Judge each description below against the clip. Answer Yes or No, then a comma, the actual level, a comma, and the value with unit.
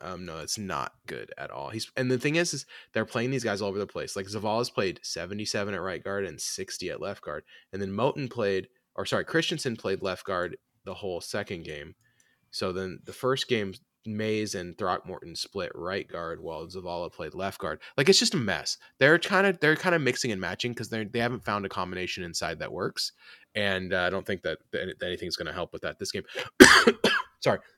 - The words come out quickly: Yes, fast, 220 wpm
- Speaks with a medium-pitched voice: No, low, 110 Hz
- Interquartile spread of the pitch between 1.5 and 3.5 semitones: No, average, 5.0 semitones